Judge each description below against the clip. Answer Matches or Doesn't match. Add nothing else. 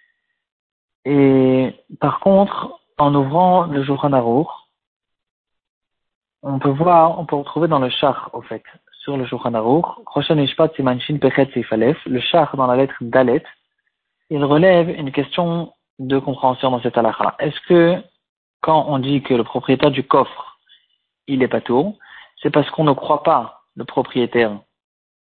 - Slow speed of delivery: Matches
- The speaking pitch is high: Doesn't match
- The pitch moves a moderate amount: Matches